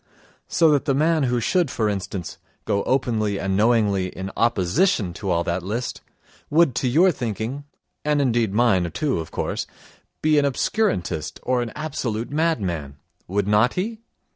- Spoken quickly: No, average, 160 wpm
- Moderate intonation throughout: No, wide, 6.9 semitones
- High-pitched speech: No, low, 115 Hz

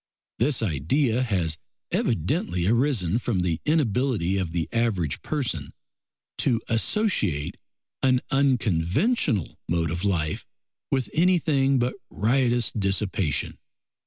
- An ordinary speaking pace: No, slow, 100 wpm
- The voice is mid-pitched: No, low, 110 Hz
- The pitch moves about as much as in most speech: No, wide, 7.4 semitones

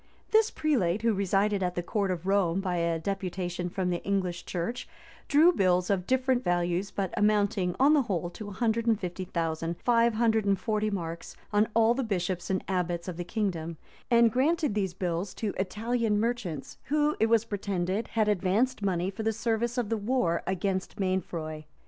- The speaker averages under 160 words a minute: No, average, 185 wpm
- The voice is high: Yes, high, 200 Hz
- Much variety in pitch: No, average, 4.2 semitones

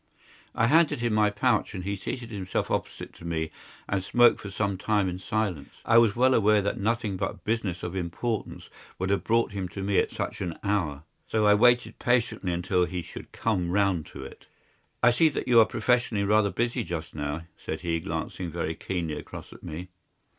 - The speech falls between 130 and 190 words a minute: No, average, 200 wpm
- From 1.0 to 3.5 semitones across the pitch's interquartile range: No, average, 4.4 semitones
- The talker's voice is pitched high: No, low, 100 Hz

